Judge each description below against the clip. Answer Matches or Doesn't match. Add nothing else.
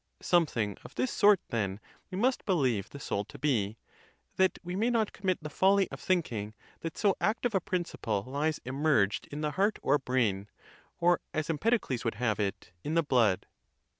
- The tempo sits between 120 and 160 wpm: Doesn't match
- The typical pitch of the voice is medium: Matches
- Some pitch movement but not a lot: Doesn't match